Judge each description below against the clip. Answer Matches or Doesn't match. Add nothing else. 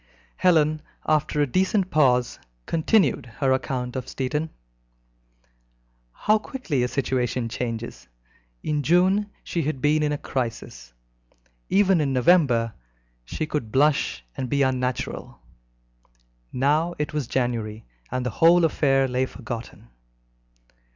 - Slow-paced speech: Matches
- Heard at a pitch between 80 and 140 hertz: Matches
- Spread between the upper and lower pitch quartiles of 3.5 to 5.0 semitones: Matches